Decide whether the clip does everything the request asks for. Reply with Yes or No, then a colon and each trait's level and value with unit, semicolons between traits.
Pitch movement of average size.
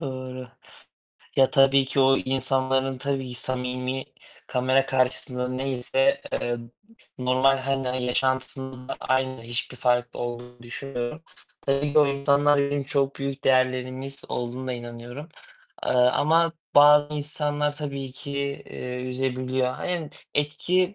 No: narrow, 1.7 semitones